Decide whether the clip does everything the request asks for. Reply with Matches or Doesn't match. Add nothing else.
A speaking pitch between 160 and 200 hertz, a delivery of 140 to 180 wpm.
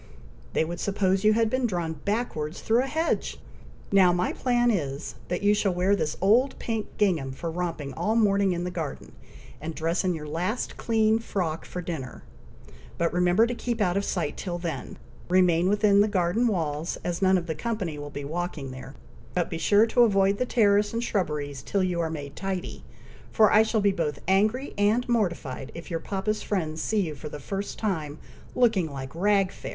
Doesn't match